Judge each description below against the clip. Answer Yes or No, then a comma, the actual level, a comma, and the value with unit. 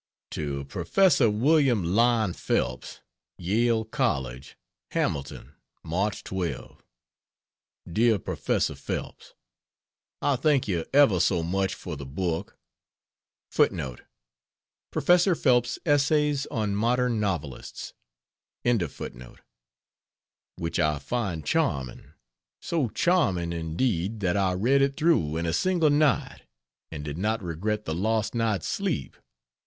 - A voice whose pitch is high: No, low, 105 Hz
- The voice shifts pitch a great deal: Yes, wide, 7.1 semitones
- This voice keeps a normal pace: No, slow, 105 wpm